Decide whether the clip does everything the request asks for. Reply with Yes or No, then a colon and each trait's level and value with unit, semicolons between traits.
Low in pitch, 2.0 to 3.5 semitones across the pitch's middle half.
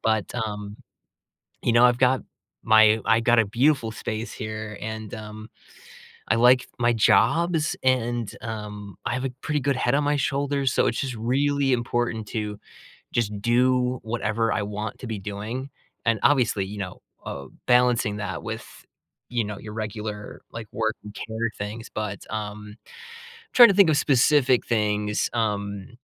Yes: low, 115 Hz; average, 2.9 semitones